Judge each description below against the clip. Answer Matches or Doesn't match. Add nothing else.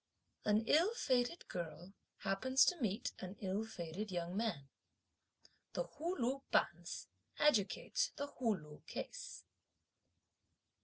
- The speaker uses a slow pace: Matches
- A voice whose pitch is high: Matches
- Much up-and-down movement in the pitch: Matches